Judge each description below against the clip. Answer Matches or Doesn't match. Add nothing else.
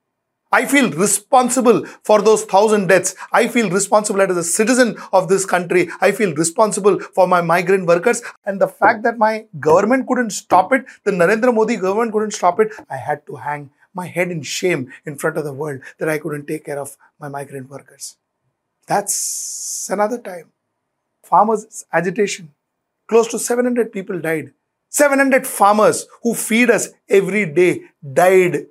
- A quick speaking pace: Doesn't match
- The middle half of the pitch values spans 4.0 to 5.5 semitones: Matches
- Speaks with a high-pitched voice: Matches